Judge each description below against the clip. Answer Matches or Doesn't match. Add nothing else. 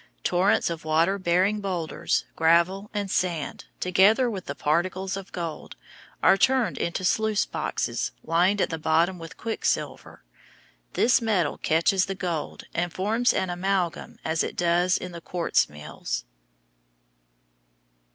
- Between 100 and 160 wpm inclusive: Matches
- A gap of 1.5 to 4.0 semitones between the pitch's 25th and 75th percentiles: Matches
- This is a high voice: Doesn't match